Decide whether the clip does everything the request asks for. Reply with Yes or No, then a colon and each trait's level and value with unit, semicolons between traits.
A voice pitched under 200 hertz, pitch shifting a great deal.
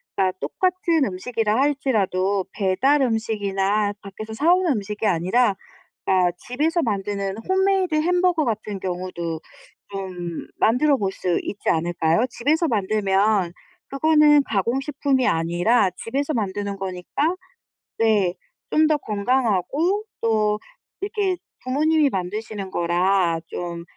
No: high, 215 Hz; wide, 7.0 semitones